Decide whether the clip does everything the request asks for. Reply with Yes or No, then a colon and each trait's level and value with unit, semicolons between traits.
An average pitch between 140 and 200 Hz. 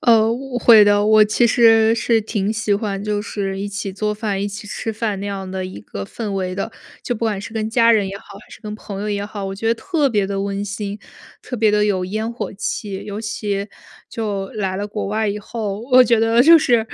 No: high, 210 Hz